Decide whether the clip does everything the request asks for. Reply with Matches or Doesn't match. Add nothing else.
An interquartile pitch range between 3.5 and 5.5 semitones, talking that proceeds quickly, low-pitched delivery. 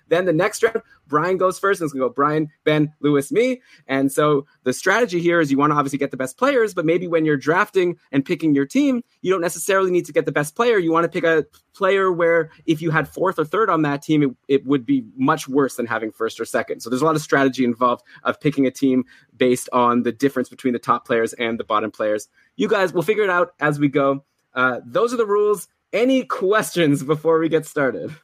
Doesn't match